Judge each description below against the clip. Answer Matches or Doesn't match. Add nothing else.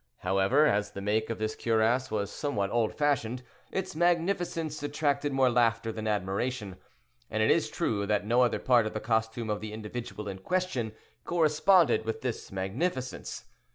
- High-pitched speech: Doesn't match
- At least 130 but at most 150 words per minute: Doesn't match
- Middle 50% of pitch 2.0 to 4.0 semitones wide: Doesn't match